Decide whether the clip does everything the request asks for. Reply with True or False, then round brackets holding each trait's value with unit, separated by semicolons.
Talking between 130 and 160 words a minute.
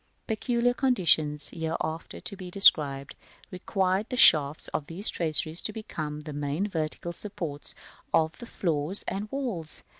True (140 wpm)